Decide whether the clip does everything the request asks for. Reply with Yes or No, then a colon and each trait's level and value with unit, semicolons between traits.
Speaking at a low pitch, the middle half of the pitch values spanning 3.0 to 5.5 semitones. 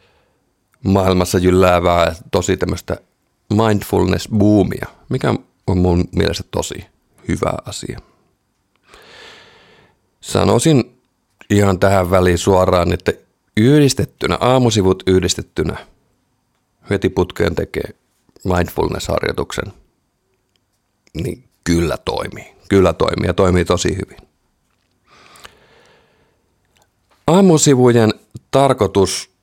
Yes: very low, 95 Hz; average, 3.4 semitones